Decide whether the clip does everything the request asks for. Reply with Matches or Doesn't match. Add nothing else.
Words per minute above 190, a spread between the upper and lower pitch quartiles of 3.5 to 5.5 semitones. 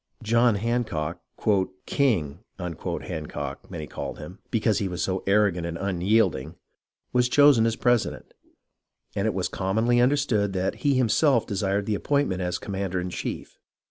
Doesn't match